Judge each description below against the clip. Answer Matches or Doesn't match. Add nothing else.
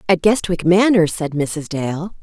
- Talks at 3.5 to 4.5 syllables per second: Matches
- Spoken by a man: Doesn't match